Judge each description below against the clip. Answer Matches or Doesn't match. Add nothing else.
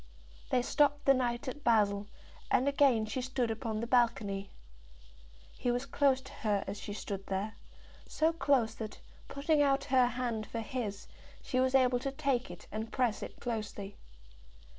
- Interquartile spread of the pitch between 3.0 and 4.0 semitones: Matches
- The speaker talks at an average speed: Matches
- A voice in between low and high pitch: Doesn't match